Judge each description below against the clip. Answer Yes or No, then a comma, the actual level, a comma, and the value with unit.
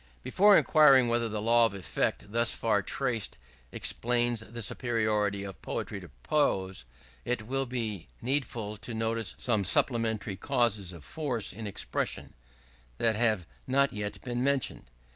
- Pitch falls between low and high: No, low, 115 Hz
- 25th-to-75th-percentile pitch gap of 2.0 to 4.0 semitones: Yes, average, 3.0 semitones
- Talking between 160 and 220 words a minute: No, average, 145 wpm